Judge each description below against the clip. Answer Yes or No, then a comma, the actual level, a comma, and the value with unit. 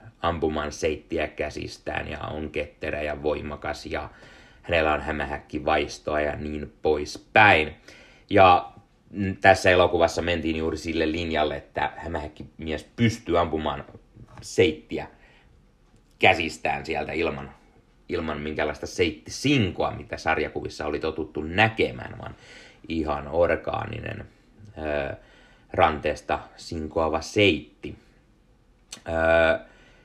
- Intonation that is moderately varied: No, narrow, 2.2 semitones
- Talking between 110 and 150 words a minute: No, slow, 95 wpm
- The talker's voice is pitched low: Yes, very low, 80 Hz